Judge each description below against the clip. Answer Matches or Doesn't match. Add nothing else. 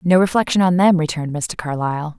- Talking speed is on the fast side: Doesn't match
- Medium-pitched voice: Matches